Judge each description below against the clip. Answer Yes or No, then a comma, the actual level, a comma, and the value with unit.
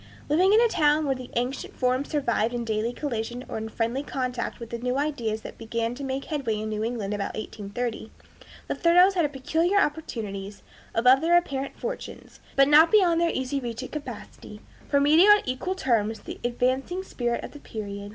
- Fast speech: No, average, 190 wpm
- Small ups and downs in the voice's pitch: No, average, 4.8 semitones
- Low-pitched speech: No, very high, 255 Hz